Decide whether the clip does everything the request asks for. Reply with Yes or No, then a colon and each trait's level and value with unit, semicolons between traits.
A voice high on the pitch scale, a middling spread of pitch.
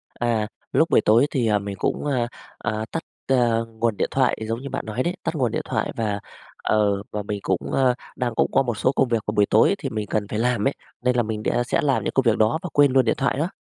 No: low, 115 Hz; average, 3.5 semitones